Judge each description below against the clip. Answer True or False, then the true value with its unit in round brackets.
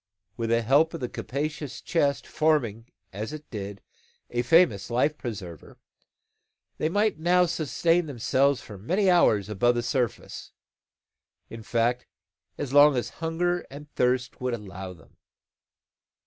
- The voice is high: False (130 Hz)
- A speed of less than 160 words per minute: True (135 wpm)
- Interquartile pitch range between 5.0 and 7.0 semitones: True (5.4 semitones)